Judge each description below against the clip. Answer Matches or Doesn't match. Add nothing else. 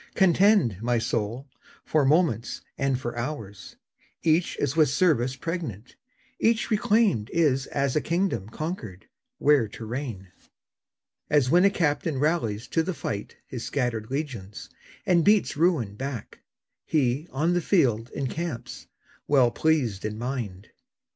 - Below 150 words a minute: Matches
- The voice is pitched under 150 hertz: Matches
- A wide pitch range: Matches